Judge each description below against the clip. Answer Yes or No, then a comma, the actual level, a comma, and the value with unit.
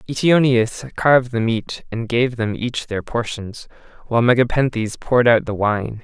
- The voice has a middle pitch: No, low, 120 Hz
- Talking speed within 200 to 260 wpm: No, average, 160 wpm